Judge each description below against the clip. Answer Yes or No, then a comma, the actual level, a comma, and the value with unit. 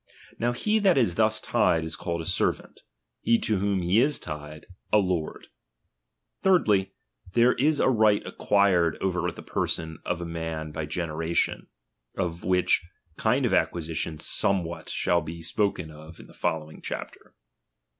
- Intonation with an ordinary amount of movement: Yes, average, 4.9 semitones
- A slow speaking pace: No, average, 155 wpm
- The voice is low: Yes, very low, 90 Hz